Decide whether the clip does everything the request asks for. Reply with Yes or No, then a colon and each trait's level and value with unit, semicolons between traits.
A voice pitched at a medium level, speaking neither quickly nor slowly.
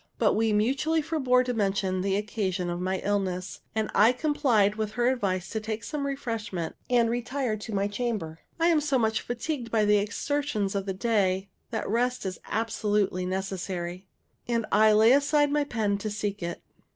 No: high, 215 Hz; average, 180 wpm